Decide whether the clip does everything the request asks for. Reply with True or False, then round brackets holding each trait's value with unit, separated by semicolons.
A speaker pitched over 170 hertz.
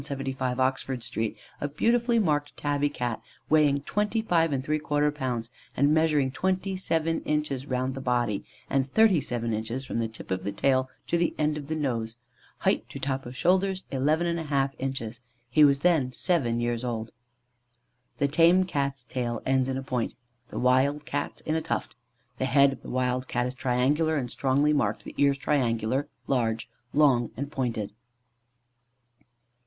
False (135 Hz)